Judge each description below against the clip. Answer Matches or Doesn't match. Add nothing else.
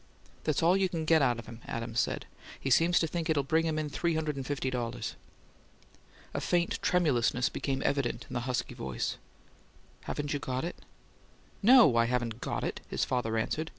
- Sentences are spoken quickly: Doesn't match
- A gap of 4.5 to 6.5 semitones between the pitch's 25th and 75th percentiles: Matches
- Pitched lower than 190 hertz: Matches